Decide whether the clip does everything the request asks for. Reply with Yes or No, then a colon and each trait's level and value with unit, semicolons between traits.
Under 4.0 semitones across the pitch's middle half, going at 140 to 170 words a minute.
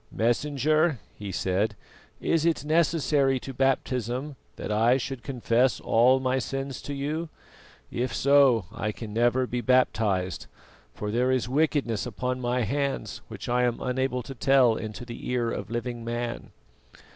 Yes: narrow, 2.6 semitones; average, 150 wpm